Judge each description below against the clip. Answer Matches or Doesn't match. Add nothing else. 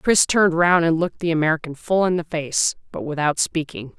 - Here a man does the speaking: Doesn't match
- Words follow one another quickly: Matches